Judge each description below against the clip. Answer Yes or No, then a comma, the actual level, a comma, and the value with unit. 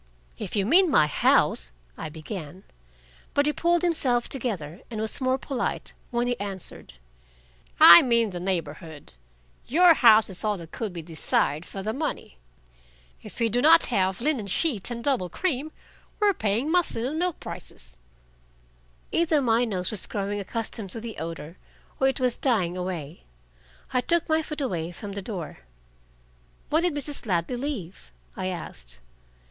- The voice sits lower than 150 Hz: No, high, 220 Hz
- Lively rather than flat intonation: Yes, wide, 7.2 semitones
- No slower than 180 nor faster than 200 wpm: No, average, 165 wpm